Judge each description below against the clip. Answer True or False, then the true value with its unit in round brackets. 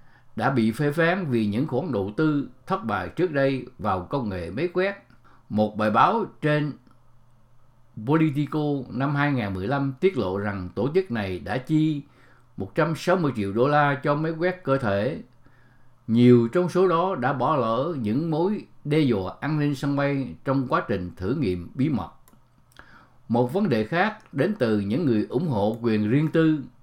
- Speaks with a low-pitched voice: True (130 Hz)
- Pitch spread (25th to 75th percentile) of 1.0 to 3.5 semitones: False (4.2 semitones)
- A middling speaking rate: True (170 wpm)